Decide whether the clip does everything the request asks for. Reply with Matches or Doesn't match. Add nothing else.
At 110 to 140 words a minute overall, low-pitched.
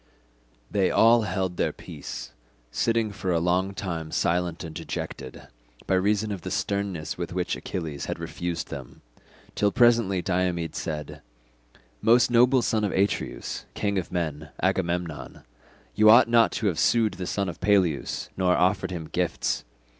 Doesn't match